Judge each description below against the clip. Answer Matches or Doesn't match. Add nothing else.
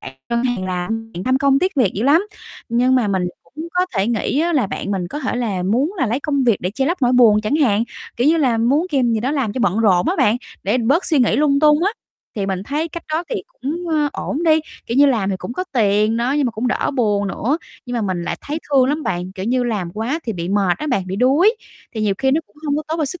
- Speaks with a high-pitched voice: Matches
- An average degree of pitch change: Doesn't match